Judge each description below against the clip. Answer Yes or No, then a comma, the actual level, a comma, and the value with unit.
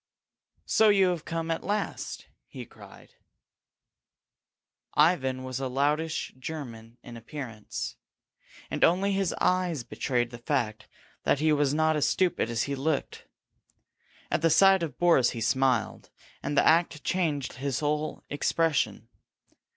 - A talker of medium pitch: Yes, medium, 150 Hz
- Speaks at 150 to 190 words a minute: No, slow, 135 wpm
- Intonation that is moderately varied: Yes, average, 4.3 semitones